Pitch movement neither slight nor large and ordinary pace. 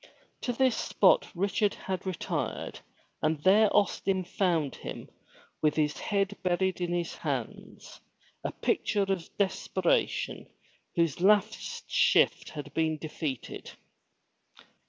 No: average, 3.9 semitones; slow, 115 wpm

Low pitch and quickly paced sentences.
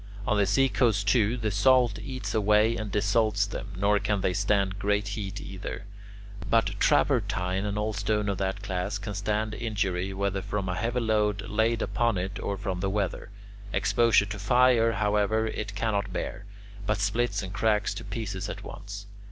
No: low, 105 Hz; average, 175 wpm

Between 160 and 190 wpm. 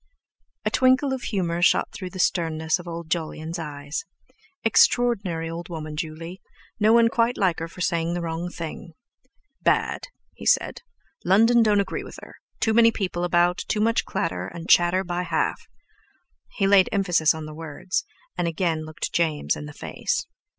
Yes: average, 165 wpm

